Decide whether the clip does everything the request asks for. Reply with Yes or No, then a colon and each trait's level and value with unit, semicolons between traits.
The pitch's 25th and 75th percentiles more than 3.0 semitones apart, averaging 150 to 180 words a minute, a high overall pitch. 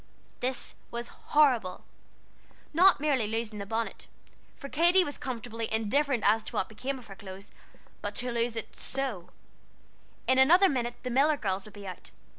Yes: average, 4.4 semitones; average, 165 wpm; high, 240 Hz